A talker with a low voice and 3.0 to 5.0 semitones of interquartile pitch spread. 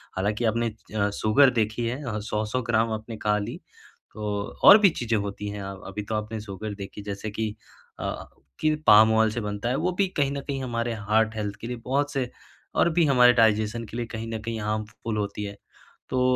No: low, 110 Hz; narrow, 2.4 semitones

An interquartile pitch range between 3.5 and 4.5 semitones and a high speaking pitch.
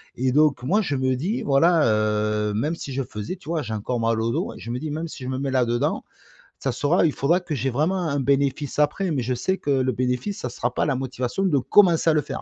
No: average, 4.1 semitones; low, 135 Hz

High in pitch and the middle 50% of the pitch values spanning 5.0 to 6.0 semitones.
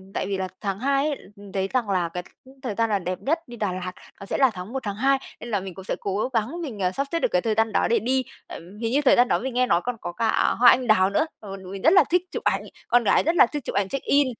Yes: high, 225 Hz; average, 5.3 semitones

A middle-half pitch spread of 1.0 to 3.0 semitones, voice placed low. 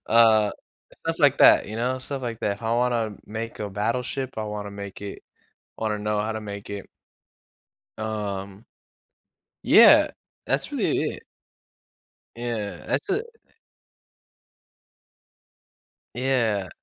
Yes: narrow, 2.4 semitones; low, 110 Hz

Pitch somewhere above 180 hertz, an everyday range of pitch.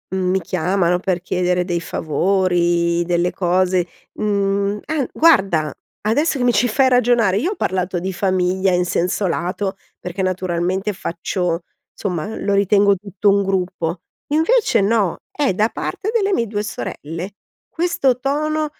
Yes: high, 190 Hz; average, 3.6 semitones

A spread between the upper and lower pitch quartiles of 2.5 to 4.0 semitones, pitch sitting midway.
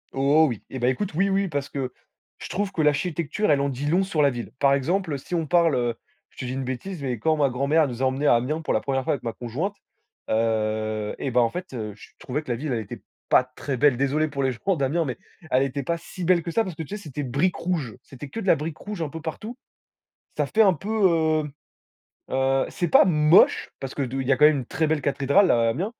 No: average, 4.6 semitones; medium, 145 Hz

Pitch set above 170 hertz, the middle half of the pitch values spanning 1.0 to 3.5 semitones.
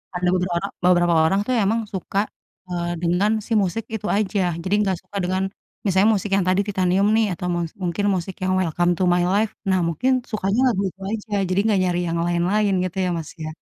Yes: medium, 185 Hz; narrow, 2.5 semitones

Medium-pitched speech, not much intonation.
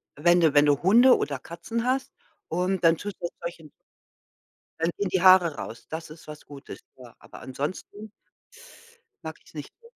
No: medium, 170 Hz; average, 4.1 semitones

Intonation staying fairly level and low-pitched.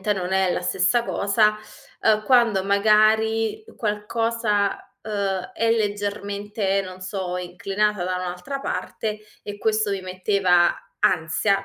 No: narrow, 2.3 semitones; high, 205 Hz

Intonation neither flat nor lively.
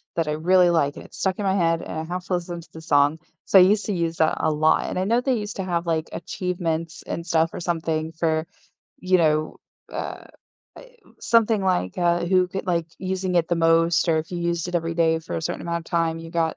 No: narrow, 2.1 semitones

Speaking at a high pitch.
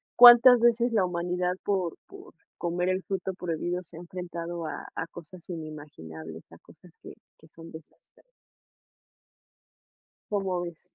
No: medium, 175 Hz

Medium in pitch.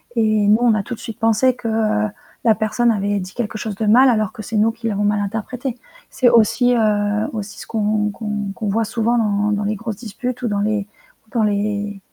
No: high, 215 Hz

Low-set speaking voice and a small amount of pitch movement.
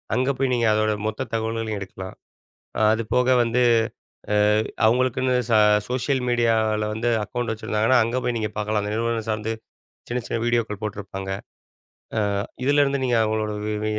Yes: low, 115 Hz; narrow, 2.3 semitones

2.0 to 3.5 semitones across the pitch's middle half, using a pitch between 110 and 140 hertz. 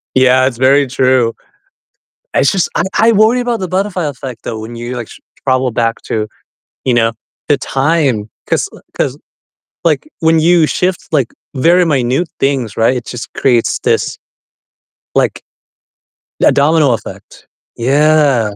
No: average, 5.1 semitones; low, 135 Hz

